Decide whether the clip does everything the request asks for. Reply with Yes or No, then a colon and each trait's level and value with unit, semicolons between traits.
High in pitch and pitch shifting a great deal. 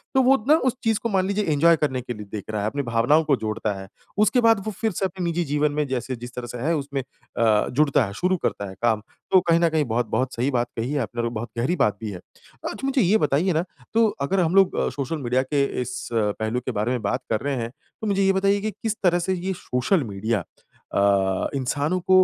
No: medium, 140 Hz; wide, 7.9 semitones